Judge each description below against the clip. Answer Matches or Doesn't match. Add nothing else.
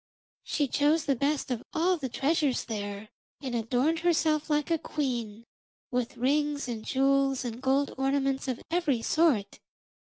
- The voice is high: Matches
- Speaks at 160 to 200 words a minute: Doesn't match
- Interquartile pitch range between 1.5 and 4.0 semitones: Matches